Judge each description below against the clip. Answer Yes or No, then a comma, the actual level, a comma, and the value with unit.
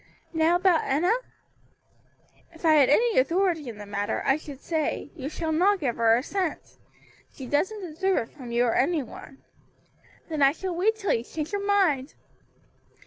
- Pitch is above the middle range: Yes, very high, 315 Hz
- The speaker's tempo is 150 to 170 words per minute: No, average, 180 wpm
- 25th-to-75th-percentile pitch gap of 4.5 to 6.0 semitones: Yes, wide, 5.6 semitones